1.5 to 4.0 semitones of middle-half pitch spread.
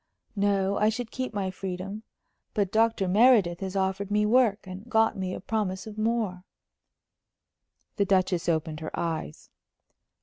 Yes: average, 2.8 semitones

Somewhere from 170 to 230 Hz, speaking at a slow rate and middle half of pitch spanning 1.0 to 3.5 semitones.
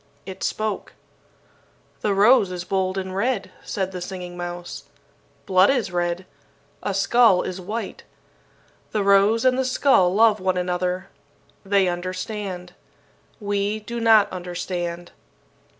Yes: high, 190 Hz; slow, 125 wpm; average, 2.9 semitones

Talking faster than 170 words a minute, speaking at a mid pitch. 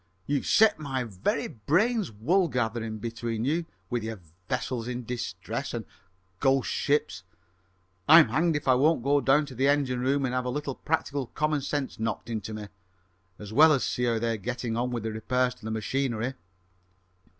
No: average, 180 wpm; low, 125 Hz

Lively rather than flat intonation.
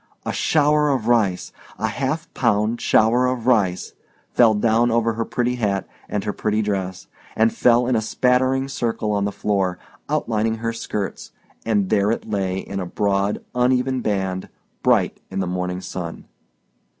No: average, 3.7 semitones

